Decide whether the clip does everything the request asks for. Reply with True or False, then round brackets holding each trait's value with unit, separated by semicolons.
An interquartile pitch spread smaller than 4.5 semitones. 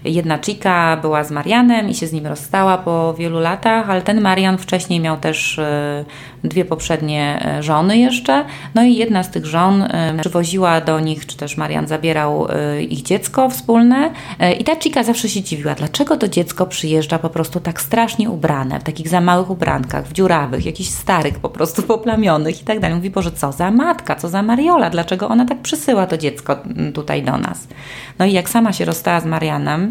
False (5.3 semitones)